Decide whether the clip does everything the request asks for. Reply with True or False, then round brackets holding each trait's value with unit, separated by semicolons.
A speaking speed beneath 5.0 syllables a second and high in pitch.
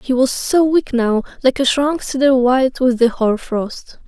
True (4.3 syllables/s; 255 Hz)